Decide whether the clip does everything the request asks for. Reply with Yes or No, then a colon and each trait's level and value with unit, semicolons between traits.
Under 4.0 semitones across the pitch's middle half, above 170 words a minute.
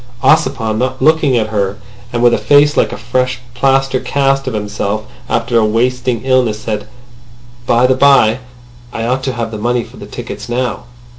Yes: average, 2.8 semitones; average, 180 wpm